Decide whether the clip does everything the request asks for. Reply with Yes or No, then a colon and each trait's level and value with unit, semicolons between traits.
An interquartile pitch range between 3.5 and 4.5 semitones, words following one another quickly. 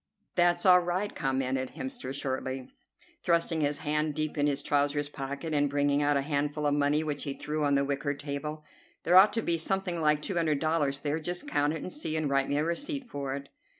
No: average, 2.7 semitones; fast, 220 wpm